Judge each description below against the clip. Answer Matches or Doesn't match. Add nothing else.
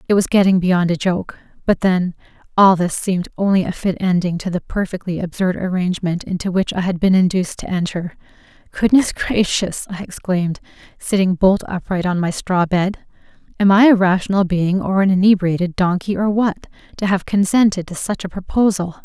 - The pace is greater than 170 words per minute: Matches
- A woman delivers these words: Matches